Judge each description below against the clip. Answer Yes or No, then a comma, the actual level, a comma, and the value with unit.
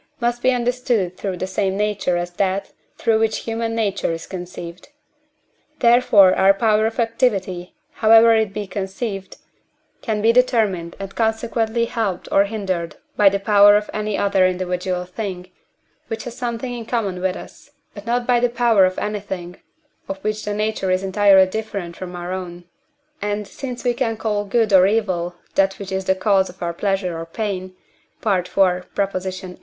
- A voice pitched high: Yes, high, 200 Hz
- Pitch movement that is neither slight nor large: Yes, average, 3.2 semitones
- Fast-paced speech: No, average, 165 wpm